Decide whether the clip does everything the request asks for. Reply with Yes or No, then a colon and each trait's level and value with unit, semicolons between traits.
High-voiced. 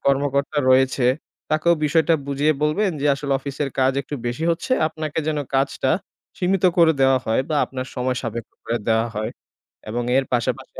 No: medium, 140 Hz